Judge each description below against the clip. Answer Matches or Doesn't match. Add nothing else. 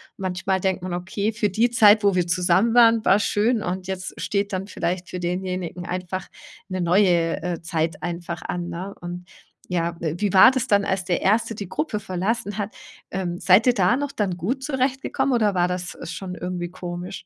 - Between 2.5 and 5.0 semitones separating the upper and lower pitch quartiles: Matches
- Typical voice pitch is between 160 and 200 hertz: Matches